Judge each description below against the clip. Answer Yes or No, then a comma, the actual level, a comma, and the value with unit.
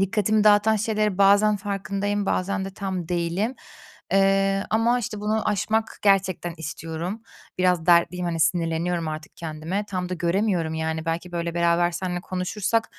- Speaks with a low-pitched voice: No, medium, 185 Hz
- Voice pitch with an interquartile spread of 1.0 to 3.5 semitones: Yes, average, 3.2 semitones